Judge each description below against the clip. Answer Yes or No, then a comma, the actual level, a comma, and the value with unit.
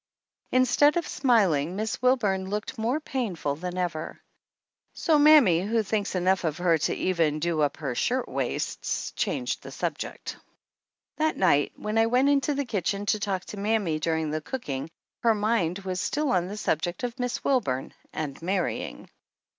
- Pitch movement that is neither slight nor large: No, wide, 6.6 semitones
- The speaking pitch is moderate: No, high, 195 Hz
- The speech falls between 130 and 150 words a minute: No, average, 170 wpm